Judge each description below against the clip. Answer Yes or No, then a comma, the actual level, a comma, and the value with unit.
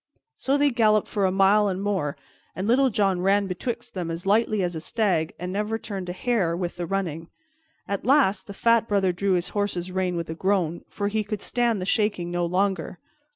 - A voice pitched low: No, high, 195 Hz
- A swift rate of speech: Yes, fast, 210 wpm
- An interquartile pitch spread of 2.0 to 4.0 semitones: Yes, average, 2.9 semitones